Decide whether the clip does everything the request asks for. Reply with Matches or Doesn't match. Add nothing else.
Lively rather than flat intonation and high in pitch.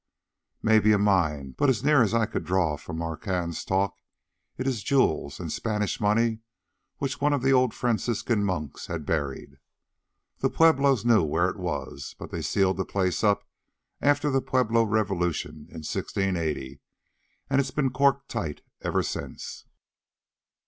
Doesn't match